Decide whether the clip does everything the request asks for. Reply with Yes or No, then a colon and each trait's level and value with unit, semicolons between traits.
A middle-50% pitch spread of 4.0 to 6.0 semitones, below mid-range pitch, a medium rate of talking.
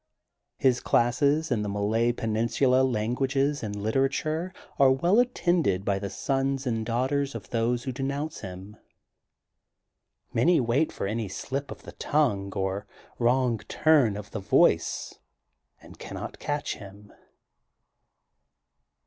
No: average, 4.8 semitones; low, 120 Hz; slow, 125 wpm